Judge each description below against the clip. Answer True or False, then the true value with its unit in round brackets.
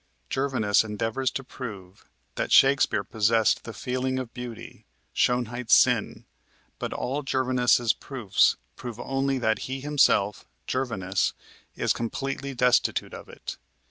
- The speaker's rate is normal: False (120 wpm)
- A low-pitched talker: True (125 Hz)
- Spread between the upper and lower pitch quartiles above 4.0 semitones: False (3.2 semitones)